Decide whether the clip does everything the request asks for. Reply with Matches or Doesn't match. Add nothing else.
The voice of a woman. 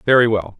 Doesn't match